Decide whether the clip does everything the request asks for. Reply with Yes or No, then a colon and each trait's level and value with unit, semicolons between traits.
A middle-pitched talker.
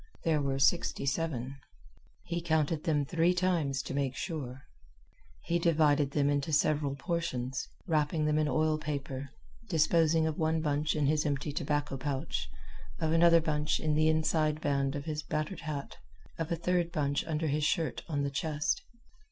Yes: medium, 150 Hz